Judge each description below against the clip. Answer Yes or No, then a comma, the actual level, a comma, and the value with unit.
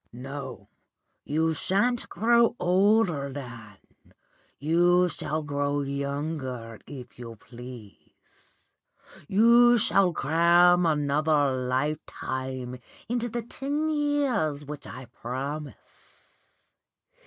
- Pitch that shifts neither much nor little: No, wide, 6.4 semitones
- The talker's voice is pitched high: No, medium, 150 Hz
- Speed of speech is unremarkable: No, slow, 85 wpm